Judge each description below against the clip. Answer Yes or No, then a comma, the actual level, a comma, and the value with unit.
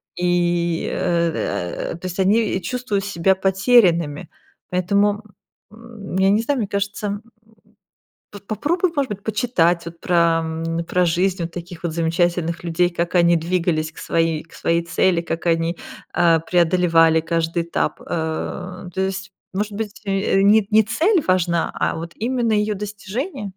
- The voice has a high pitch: No, medium, 180 Hz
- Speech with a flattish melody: No, average, 3.4 semitones